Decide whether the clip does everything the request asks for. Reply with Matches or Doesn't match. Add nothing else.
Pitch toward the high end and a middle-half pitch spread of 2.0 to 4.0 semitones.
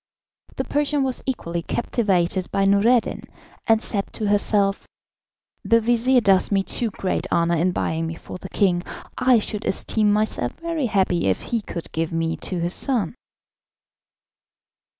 Doesn't match